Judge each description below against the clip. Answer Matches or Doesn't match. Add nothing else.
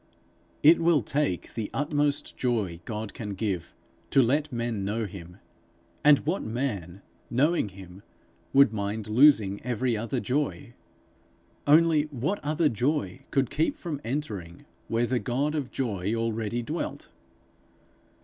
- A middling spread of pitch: Doesn't match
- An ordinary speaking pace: Doesn't match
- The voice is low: Matches